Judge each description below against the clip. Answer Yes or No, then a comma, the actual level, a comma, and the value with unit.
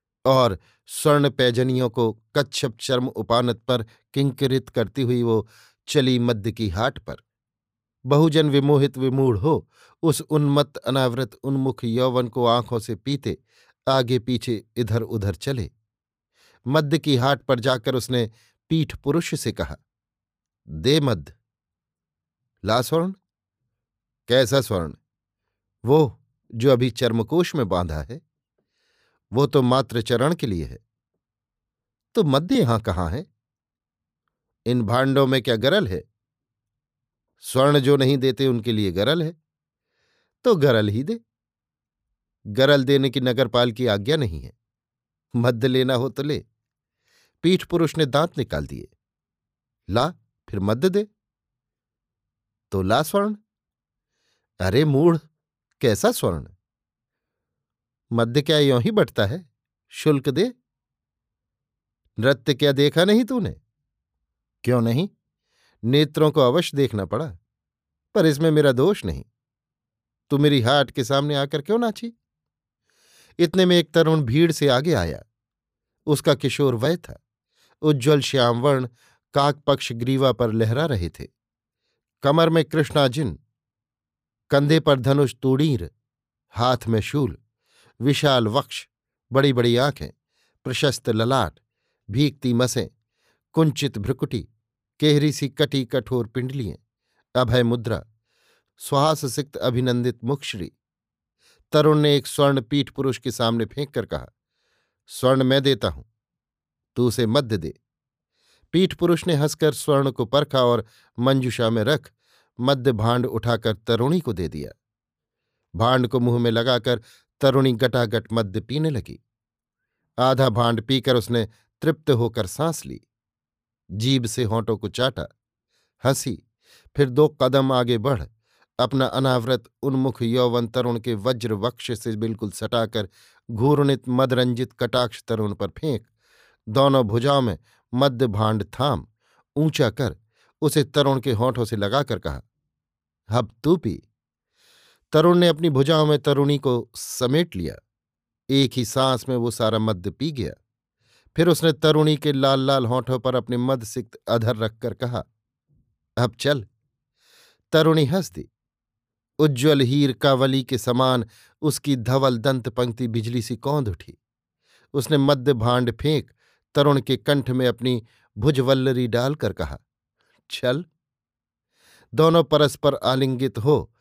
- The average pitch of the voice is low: Yes, low, 130 Hz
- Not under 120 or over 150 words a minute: Yes, average, 130 wpm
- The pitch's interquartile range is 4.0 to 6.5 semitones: No, average, 3.6 semitones